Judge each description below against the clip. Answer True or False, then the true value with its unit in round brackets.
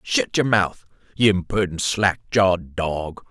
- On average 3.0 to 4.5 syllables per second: True (4.0 syllables/s)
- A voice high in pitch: False (95 Hz)